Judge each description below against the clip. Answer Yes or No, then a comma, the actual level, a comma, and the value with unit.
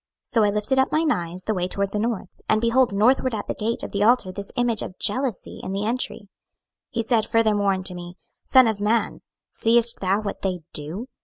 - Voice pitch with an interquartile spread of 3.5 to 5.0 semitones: No, average, 3.1 semitones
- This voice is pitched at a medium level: No, high, 215 Hz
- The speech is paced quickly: Yes, fast, 220 wpm